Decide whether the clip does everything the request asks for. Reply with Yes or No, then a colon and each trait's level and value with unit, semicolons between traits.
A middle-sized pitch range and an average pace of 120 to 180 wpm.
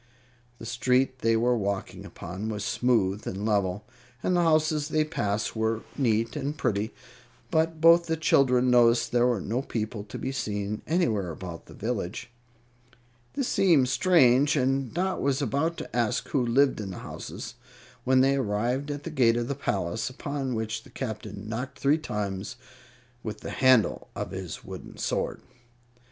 Yes: average, 4.7 semitones; average, 165 wpm